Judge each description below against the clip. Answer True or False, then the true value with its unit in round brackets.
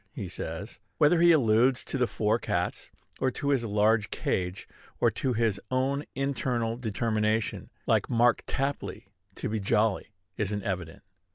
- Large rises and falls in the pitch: False (3.8 semitones)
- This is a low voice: True (115 Hz)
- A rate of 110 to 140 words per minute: False (150 wpm)